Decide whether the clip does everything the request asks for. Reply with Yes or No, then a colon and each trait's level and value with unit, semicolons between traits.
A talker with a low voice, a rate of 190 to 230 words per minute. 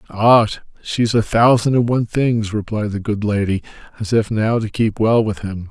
Yes: low, 110 Hz; average, 200 wpm